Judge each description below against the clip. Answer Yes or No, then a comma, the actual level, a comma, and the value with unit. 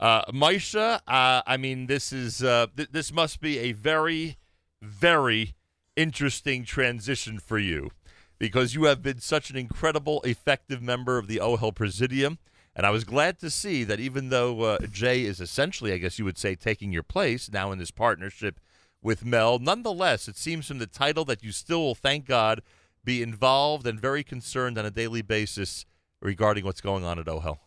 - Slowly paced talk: No, average, 185 wpm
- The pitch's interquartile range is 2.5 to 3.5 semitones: No, average, 5.0 semitones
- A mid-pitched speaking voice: No, low, 120 Hz